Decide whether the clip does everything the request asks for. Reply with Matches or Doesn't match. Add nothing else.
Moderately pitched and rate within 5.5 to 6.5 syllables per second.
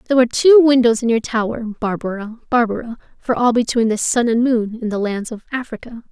Doesn't match